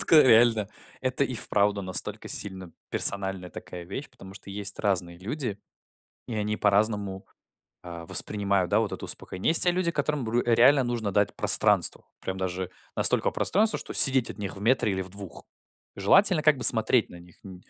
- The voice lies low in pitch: Yes, low, 105 Hz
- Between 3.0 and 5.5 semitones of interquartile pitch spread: Yes, average, 4.4 semitones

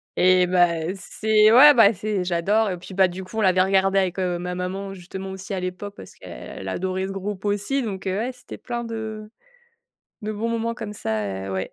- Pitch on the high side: Yes, high, 195 Hz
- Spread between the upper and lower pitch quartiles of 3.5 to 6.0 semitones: No, average, 2.8 semitones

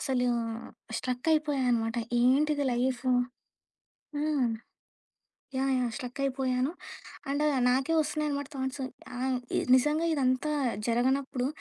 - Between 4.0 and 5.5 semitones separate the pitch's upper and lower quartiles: No, narrow, 2.4 semitones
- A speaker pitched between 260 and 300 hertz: Yes, very high, 265 Hz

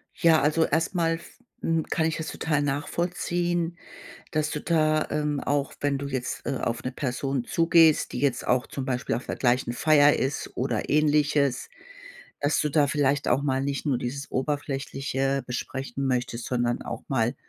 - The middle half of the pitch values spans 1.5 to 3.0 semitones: Yes, average, 2.7 semitones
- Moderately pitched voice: Yes, medium, 145 Hz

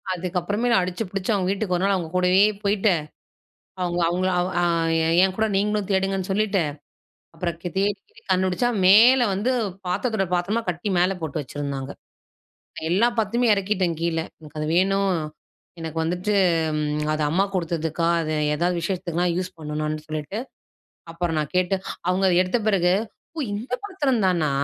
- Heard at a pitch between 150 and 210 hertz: Yes, medium, 185 Hz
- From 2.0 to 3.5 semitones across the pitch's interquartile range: Yes, average, 3.0 semitones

